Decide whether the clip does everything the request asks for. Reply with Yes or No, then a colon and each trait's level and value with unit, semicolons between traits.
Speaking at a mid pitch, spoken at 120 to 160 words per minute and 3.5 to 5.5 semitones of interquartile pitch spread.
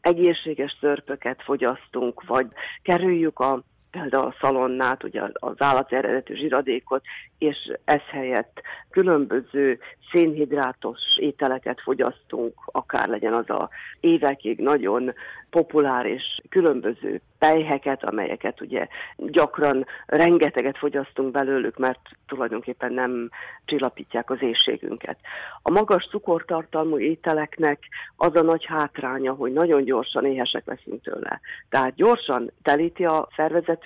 No: medium, 145 Hz; average, 110 wpm; average, 4.0 semitones